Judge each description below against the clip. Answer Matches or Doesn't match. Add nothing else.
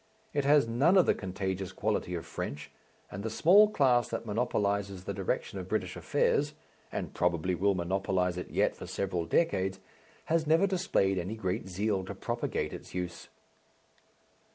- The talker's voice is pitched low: Matches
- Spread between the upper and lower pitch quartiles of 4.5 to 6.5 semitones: Matches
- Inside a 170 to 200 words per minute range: Doesn't match